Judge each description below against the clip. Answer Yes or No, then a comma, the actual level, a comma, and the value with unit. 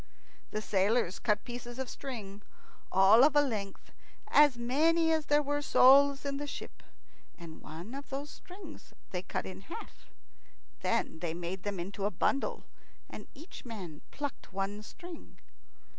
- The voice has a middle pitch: No, high, 240 Hz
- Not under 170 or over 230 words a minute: No, average, 155 wpm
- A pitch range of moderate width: No, wide, 6.7 semitones